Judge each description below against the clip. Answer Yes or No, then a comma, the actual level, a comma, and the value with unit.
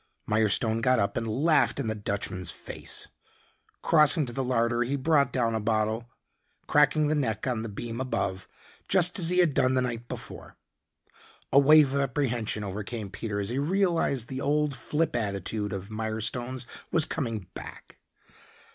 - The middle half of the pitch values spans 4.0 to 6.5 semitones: Yes, average, 4.5 semitones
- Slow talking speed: No, average, 165 wpm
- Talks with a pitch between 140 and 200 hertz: No, low, 120 Hz